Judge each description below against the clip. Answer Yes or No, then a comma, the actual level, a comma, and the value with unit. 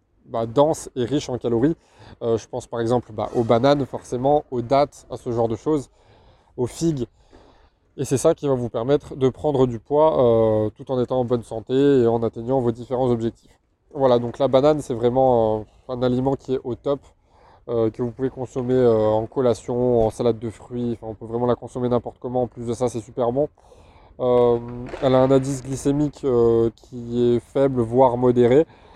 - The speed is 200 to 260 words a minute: Yes, average, 205 wpm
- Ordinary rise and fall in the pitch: No, narrow, 2.3 semitones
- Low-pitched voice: Yes, low, 125 Hz